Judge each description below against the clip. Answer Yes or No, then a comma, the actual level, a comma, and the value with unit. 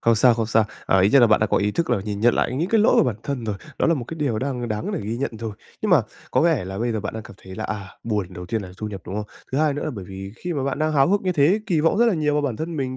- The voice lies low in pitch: Yes, low, 120 Hz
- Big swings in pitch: Yes, wide, 6.3 semitones